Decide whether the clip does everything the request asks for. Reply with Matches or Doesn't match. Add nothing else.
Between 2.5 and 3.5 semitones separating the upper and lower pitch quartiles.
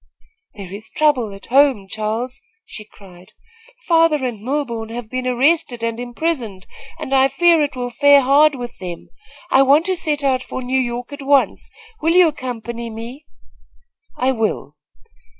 Doesn't match